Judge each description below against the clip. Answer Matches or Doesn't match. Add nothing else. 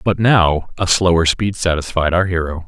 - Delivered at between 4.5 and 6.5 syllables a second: Matches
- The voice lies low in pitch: Matches